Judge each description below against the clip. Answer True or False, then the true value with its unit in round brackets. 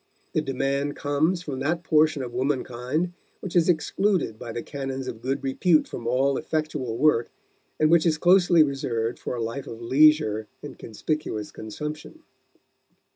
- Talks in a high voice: False (140 Hz)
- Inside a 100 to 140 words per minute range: False (155 wpm)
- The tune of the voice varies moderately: True (4.1 semitones)